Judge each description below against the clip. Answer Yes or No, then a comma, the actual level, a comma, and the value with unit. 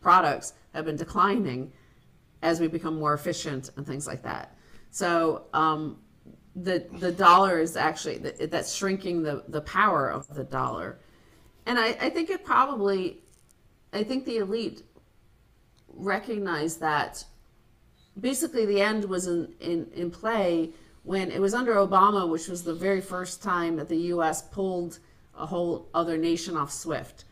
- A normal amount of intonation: Yes, average, 3.7 semitones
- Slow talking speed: No, average, 155 wpm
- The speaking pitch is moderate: Yes, medium, 175 Hz